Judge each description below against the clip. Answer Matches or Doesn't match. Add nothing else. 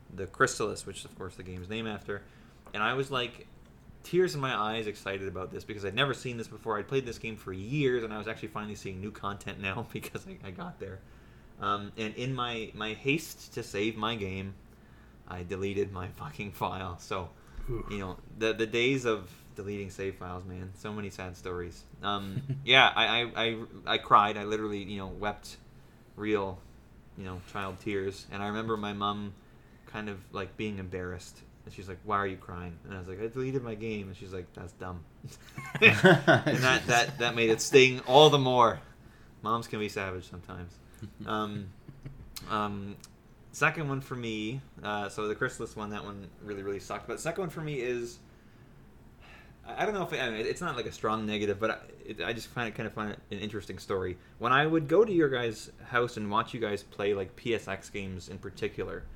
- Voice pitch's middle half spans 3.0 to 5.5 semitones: Matches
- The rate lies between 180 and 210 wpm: Matches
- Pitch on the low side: Matches